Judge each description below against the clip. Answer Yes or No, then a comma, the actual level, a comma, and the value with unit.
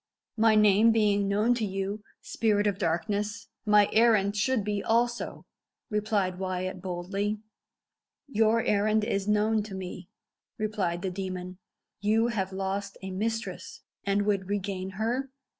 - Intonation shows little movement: Yes, narrow, 2.1 semitones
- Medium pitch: No, high, 205 Hz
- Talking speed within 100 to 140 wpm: Yes, slow, 135 wpm